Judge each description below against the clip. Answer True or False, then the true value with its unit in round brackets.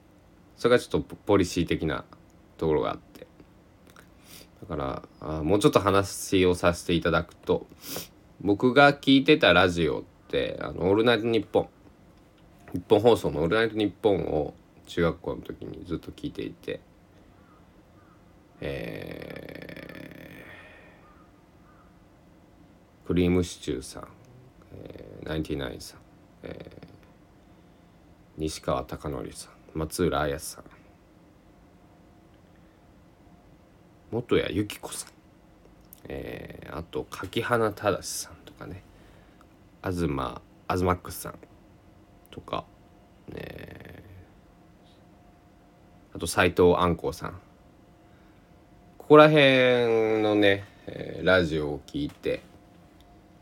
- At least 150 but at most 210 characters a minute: True (190 characters per minute)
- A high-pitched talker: False (90 Hz)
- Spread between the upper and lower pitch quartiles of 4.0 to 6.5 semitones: False (3.5 semitones)